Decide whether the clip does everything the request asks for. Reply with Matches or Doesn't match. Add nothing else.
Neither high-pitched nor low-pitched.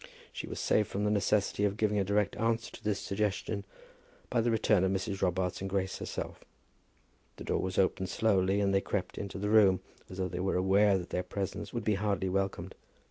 Doesn't match